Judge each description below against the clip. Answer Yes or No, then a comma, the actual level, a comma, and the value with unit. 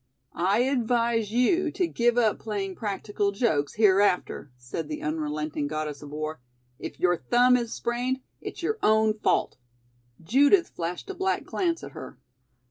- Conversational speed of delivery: Yes, average, 150 wpm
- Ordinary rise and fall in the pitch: No, wide, 7.3 semitones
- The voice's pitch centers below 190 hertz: No, high, 215 Hz